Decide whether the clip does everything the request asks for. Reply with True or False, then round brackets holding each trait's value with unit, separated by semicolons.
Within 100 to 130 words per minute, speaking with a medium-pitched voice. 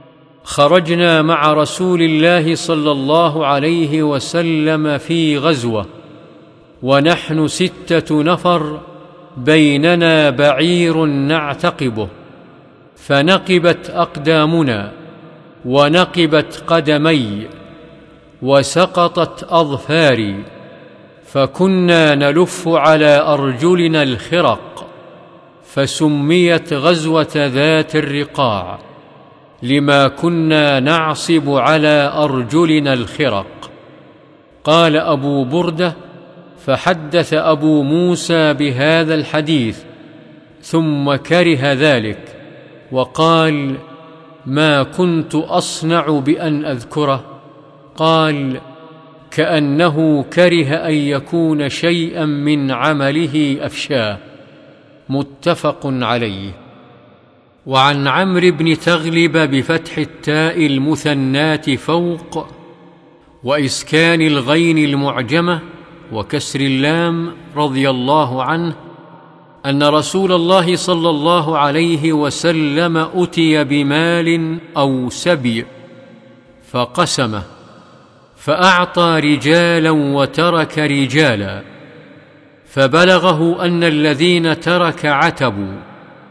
False (70 wpm; 155 Hz)